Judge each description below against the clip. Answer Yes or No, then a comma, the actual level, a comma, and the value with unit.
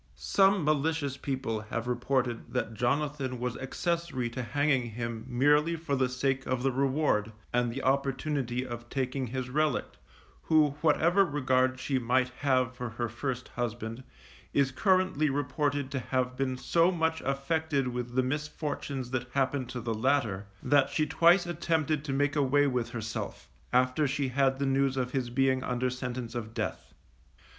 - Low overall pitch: Yes, low, 130 Hz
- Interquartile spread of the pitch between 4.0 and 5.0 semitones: No, average, 2.7 semitones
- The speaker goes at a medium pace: Yes, average, 160 wpm